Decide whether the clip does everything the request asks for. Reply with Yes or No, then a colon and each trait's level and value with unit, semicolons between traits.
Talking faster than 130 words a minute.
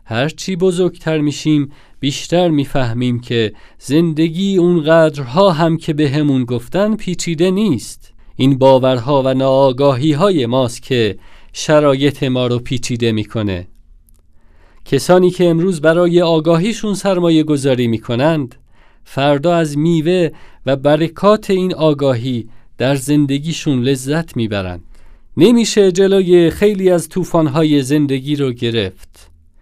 No: average, 110 wpm